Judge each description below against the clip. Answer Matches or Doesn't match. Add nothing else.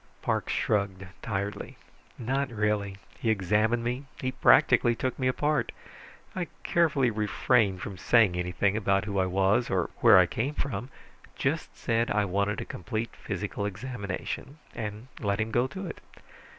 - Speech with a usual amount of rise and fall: Matches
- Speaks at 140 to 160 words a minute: Matches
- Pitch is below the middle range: Matches